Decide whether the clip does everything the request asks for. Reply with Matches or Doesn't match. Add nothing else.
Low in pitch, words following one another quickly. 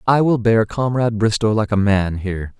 Matches